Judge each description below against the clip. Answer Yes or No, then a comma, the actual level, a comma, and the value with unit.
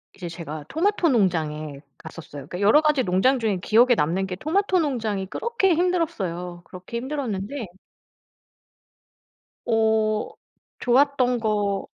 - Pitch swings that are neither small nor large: No, wide, 7.6 semitones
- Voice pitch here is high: Yes, high, 220 Hz